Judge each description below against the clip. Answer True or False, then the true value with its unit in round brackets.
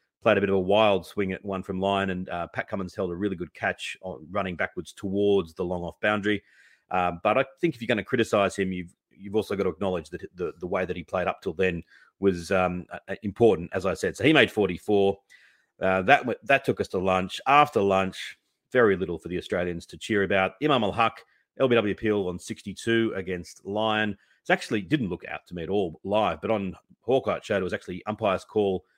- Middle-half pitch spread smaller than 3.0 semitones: True (2.6 semitones)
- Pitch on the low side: True (100 Hz)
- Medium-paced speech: False (220 wpm)